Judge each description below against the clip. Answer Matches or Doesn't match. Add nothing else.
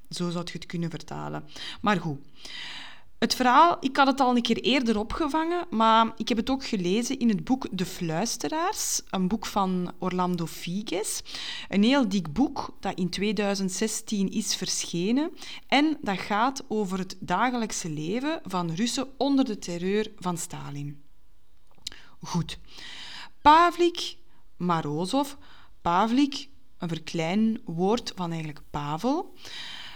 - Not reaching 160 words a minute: Matches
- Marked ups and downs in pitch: Matches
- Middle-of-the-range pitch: Doesn't match